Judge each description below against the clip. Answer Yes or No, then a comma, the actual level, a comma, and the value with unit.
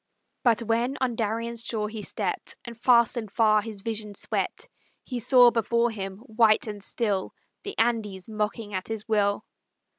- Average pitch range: No, narrow, 2.0 semitones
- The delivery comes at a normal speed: Yes, average, 160 wpm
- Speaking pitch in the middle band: No, high, 225 Hz